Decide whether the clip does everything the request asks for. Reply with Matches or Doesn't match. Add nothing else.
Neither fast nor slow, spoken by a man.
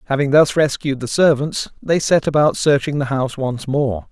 Matches